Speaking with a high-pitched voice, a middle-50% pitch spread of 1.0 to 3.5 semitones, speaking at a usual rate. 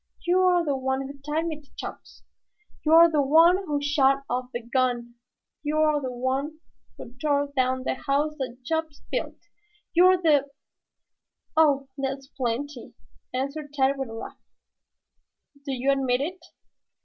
Yes: very high, 280 Hz; average, 2.8 semitones; average, 150 wpm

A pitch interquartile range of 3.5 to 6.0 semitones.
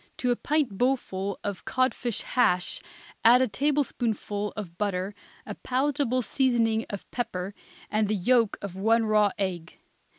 Yes: average, 4.2 semitones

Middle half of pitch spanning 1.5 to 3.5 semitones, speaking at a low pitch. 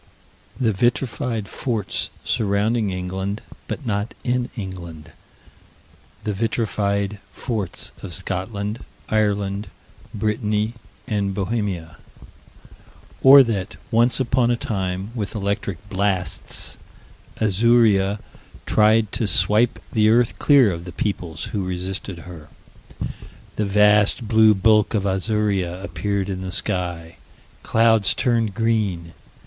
Yes: average, 2.9 semitones; low, 105 Hz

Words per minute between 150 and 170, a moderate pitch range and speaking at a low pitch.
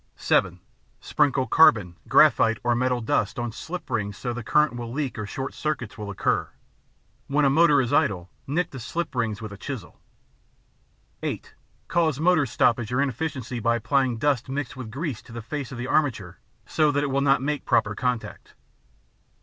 No: average, 180 wpm; average, 4.1 semitones; low, 125 Hz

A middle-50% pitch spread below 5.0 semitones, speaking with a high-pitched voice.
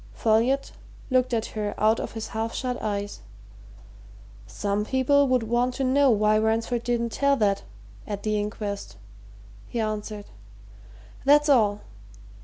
Yes: average, 3.3 semitones; high, 225 Hz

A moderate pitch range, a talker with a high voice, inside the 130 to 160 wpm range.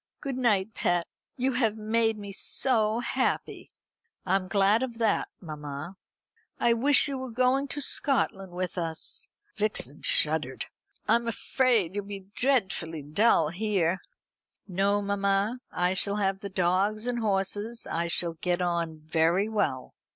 Yes: average, 4.5 semitones; high, 200 Hz; average, 145 wpm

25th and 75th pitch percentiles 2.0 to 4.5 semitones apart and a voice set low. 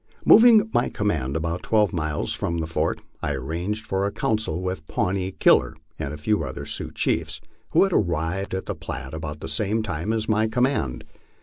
No: wide, 5.5 semitones; very low, 90 Hz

